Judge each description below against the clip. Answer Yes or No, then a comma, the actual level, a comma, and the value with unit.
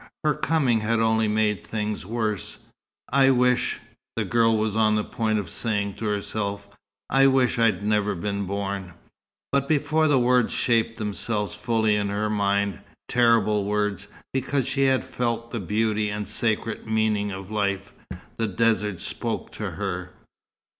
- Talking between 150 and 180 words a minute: Yes, average, 155 wpm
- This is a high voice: No, low, 110 Hz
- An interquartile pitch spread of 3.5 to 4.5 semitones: No, narrow, 2.5 semitones